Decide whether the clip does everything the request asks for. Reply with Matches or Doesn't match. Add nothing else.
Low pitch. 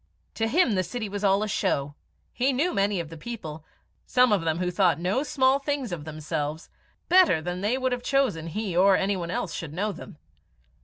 Doesn't match